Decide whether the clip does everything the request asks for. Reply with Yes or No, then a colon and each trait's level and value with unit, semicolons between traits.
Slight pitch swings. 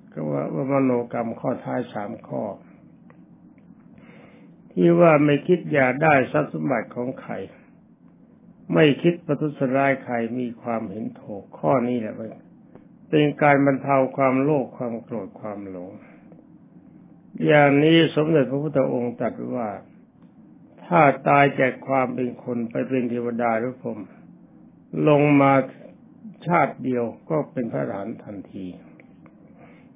No: average, 3.6 semitones